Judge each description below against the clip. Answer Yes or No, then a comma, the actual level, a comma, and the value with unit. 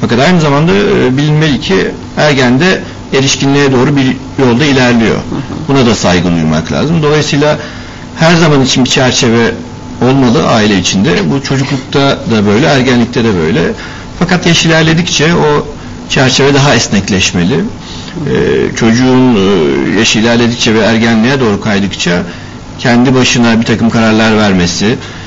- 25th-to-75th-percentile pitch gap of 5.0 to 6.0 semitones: No, average, 3.7 semitones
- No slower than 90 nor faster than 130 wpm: Yes, average, 125 wpm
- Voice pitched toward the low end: Yes, low, 125 Hz